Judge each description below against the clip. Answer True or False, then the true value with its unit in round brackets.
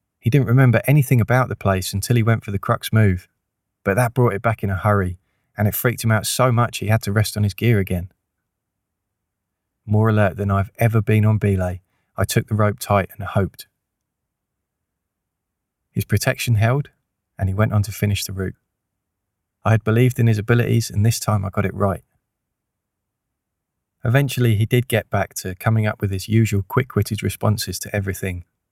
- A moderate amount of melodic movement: True (3.0 semitones)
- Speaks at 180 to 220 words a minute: True (190 wpm)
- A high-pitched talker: False (105 Hz)